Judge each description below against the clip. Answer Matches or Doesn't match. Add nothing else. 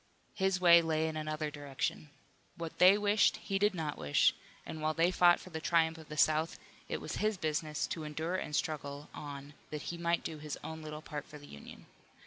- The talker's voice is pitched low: Doesn't match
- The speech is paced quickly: Matches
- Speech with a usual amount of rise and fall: Doesn't match